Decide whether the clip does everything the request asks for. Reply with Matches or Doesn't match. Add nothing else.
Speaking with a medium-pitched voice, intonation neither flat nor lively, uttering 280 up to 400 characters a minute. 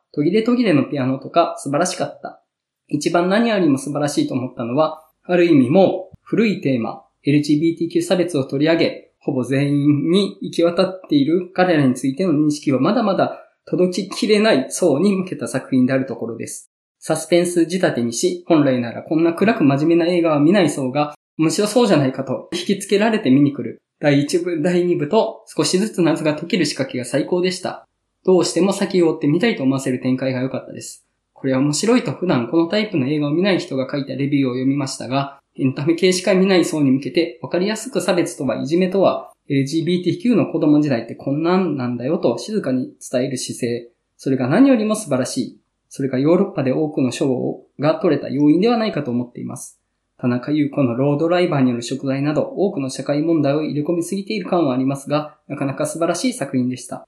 Doesn't match